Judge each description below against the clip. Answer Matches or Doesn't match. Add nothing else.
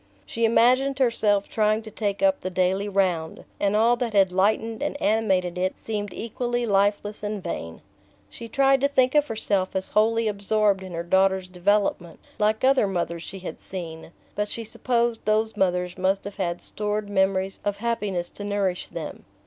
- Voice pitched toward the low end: Doesn't match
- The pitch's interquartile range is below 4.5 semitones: Matches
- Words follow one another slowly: Doesn't match